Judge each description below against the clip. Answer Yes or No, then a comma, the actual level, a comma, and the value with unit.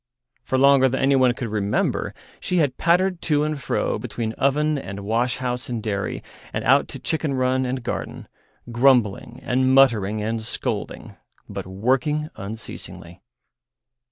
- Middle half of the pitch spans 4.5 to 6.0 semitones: No, average, 3.8 semitones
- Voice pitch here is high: No, low, 130 Hz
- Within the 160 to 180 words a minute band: No, average, 145 wpm